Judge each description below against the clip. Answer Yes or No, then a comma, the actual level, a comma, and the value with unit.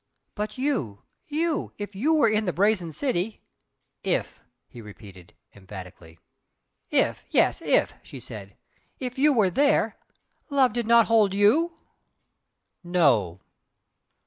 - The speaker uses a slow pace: Yes, slow, 125 wpm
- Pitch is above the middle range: Yes, high, 205 Hz